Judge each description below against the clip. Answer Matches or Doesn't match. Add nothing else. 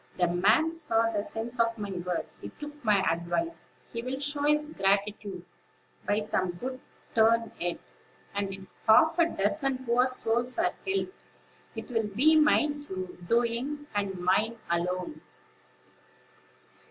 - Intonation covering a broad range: Matches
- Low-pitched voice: Doesn't match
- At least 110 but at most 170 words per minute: Matches